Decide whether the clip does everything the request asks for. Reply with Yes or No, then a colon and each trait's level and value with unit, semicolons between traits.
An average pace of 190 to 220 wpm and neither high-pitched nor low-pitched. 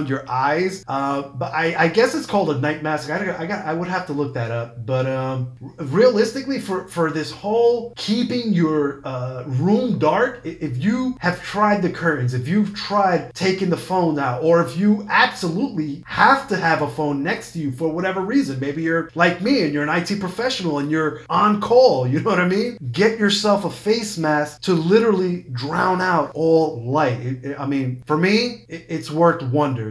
Yes: fast, 205 wpm; medium, 165 Hz